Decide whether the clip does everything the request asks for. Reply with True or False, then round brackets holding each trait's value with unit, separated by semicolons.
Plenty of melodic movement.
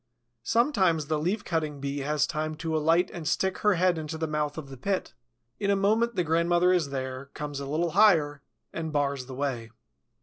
False (3.9 semitones)